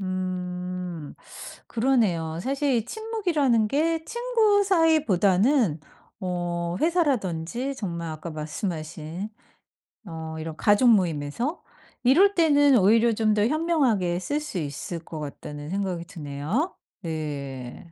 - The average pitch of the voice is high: Yes, high, 195 Hz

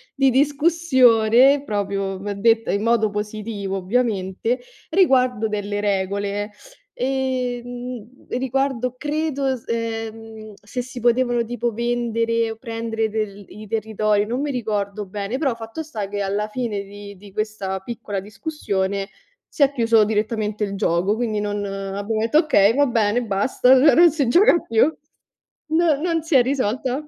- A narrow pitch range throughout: No, average, 3.7 semitones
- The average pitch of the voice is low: No, high, 225 Hz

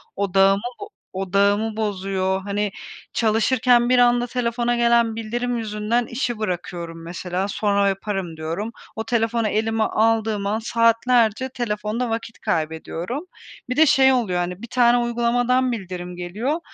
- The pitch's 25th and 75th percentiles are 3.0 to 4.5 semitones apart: Yes, average, 3.5 semitones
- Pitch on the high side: Yes, high, 220 Hz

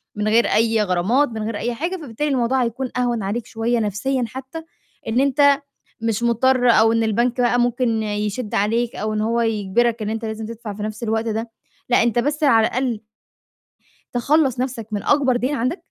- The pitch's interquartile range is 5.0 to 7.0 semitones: No, narrow, 2.6 semitones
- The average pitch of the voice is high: Yes, high, 235 Hz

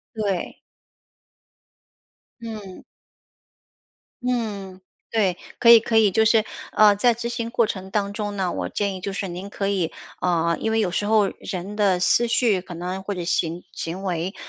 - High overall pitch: Yes, high, 200 Hz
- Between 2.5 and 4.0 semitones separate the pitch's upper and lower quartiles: Yes, average, 3.2 semitones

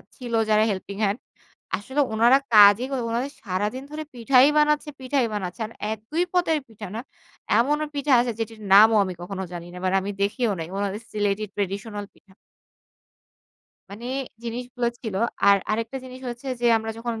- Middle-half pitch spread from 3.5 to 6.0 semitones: Yes, average, 3.8 semitones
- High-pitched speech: Yes, high, 225 Hz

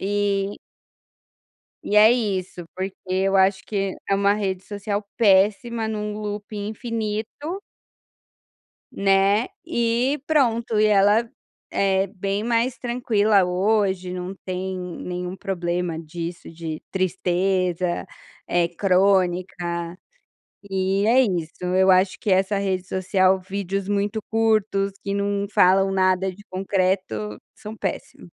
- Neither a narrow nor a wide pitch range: No, narrow, 2.3 semitones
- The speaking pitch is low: No, high, 195 Hz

